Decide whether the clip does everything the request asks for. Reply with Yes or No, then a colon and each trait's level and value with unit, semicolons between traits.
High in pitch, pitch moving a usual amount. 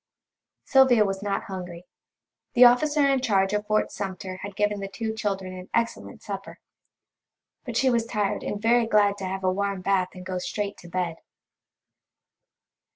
Yes: high, 200 Hz; average, 3.3 semitones